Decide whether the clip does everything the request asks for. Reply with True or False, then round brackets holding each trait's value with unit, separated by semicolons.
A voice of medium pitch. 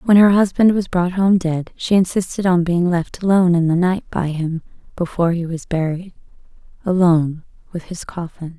True (175 Hz)